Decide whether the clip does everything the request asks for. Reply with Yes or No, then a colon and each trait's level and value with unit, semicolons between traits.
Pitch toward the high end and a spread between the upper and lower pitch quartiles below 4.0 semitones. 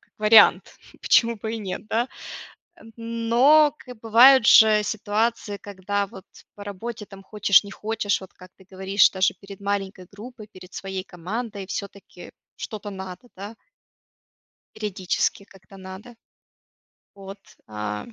Yes: high, 205 Hz; average, 2.8 semitones